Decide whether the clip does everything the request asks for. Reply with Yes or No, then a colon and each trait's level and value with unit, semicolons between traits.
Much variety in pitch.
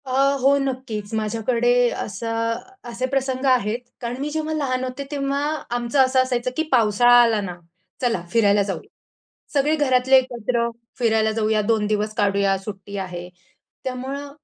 No: average, 3.4 semitones